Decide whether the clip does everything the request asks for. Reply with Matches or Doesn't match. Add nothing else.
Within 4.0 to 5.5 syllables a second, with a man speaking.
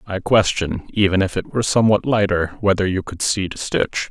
Matches